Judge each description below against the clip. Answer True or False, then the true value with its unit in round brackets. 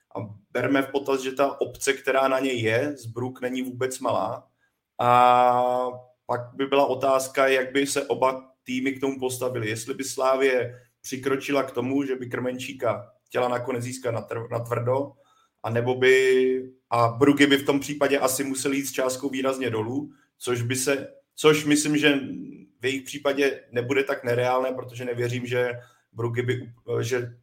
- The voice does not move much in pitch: True (1.8 semitones)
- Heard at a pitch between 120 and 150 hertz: True (130 Hz)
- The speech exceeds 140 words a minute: True (170 wpm)